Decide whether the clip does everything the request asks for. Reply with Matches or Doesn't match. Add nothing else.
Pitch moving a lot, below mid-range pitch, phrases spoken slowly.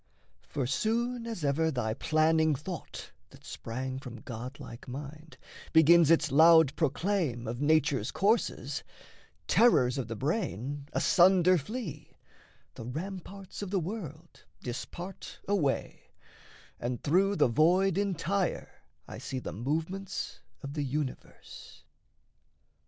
Doesn't match